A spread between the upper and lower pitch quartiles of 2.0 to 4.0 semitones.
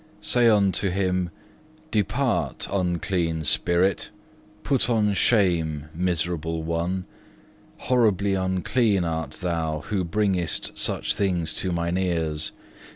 Yes: average, 3.2 semitones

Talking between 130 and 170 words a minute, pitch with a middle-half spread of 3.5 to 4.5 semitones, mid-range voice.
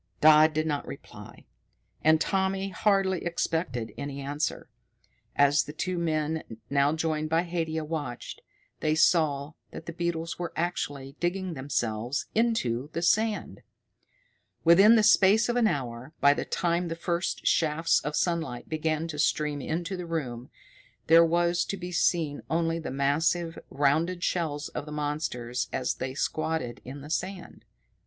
No: average, 150 wpm; average, 3.1 semitones; medium, 160 Hz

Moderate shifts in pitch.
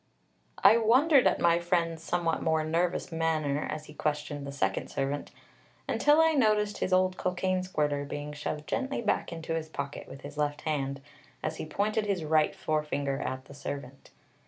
Yes: average, 4.1 semitones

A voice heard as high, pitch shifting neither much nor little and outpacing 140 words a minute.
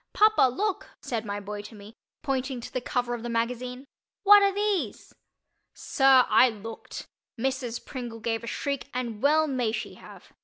Yes: very high, 250 Hz; average, 3.4 semitones; average, 175 wpm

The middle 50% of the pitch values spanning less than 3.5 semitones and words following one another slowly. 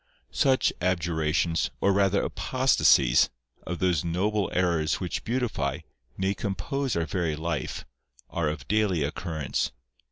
No: average, 4.0 semitones; slow, 120 wpm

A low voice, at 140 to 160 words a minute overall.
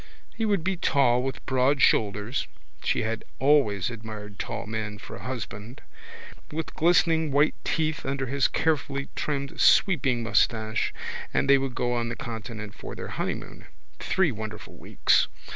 Yes: low, 130 Hz; average, 150 wpm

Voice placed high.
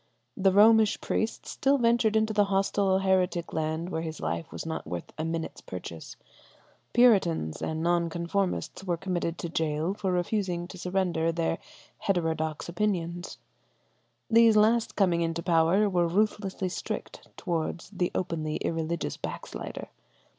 No: medium, 175 Hz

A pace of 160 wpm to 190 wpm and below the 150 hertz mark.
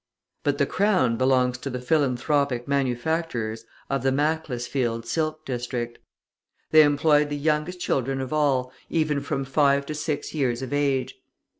No: average, 145 wpm; medium, 140 Hz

